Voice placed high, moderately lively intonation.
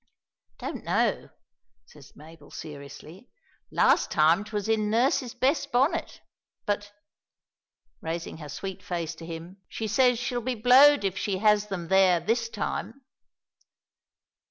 No: high, 205 Hz; wide, 6.4 semitones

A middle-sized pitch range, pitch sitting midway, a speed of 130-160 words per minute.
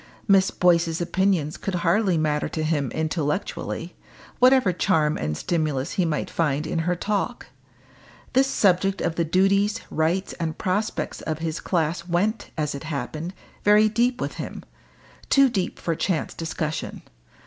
Yes: average, 3.8 semitones; medium, 170 Hz; average, 150 wpm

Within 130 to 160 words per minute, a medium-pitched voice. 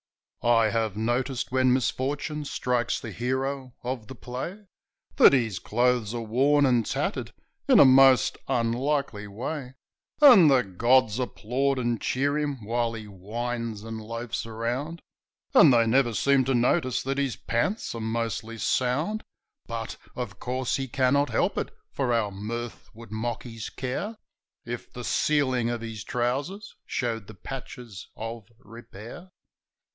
No: average, 145 wpm; low, 120 Hz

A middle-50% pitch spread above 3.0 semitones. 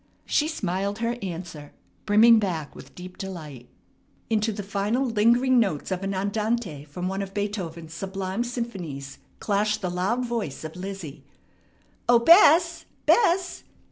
Yes: average, 4.7 semitones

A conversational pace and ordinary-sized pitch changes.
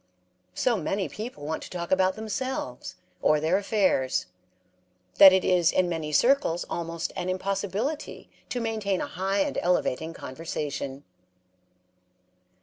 No: slow, 130 wpm; average, 4.0 semitones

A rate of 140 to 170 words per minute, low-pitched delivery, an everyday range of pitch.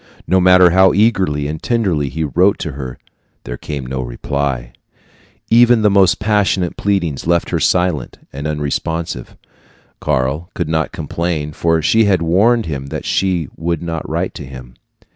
Yes: average, 160 wpm; very low, 85 Hz; average, 4.8 semitones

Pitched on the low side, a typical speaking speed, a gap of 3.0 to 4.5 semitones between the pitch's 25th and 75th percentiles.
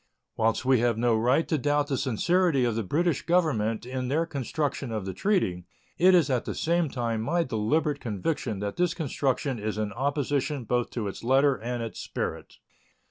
No: low, 130 Hz; average, 190 wpm; average, 5.0 semitones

